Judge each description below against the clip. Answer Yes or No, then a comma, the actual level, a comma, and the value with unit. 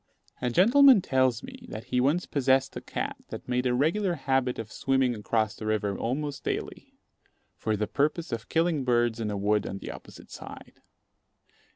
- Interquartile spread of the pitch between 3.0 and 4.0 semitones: No, average, 4.7 semitones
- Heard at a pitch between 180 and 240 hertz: No, low, 125 Hz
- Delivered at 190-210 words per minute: No, average, 180 wpm